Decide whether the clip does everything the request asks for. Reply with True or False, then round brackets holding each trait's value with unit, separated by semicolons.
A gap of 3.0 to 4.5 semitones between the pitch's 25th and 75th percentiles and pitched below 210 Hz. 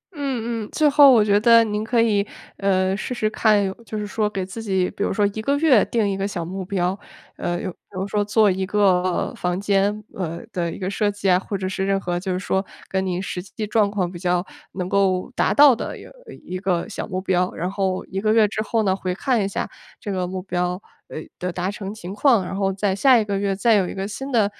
False (2.5 semitones; 195 Hz)